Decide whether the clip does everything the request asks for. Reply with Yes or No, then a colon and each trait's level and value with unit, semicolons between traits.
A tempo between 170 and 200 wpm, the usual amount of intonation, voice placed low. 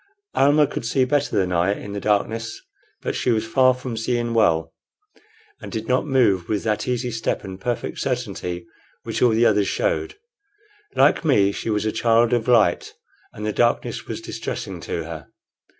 Yes: average, 180 wpm; average, 3.7 semitones; low, 115 Hz